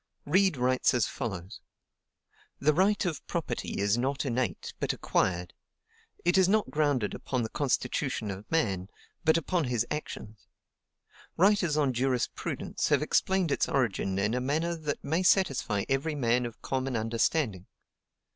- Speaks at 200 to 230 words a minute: No, average, 145 wpm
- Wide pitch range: Yes, wide, 6.0 semitones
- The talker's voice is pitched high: No, low, 135 Hz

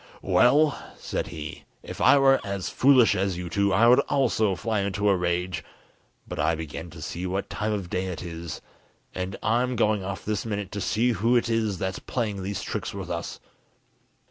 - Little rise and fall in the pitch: No, average, 3.8 semitones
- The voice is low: Yes, low, 100 Hz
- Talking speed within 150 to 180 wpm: No, average, 195 wpm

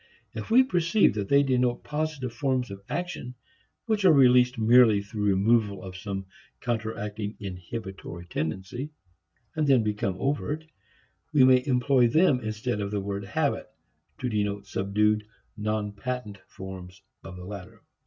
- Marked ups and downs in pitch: No, average, 4.3 semitones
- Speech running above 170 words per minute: No, average, 145 wpm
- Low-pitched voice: Yes, low, 110 Hz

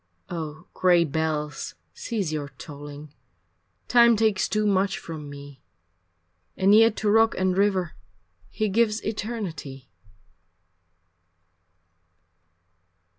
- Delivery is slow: Yes, slow, 95 wpm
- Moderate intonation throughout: No, wide, 6.0 semitones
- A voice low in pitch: No, medium, 185 Hz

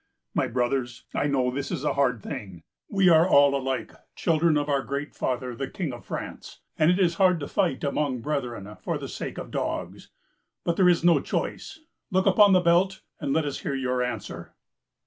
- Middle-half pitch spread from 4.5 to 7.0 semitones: Yes, average, 5.0 semitones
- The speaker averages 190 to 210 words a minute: Yes, average, 200 wpm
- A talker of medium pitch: Yes, medium, 145 Hz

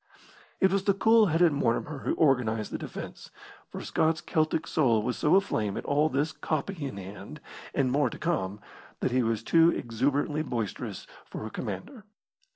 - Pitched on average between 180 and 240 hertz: No, medium, 145 Hz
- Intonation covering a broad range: Yes, wide, 6.0 semitones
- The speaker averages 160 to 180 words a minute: Yes, average, 170 wpm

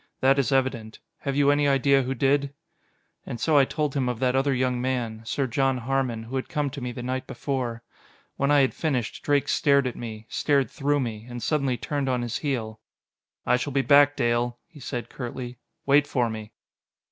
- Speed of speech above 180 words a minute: Yes, fast, 205 wpm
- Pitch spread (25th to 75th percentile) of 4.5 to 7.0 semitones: No, narrow, 2.5 semitones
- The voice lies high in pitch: No, low, 130 Hz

